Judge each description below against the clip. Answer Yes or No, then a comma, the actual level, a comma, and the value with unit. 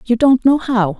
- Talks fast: Yes, fast, 240 wpm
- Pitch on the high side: Yes, high, 235 Hz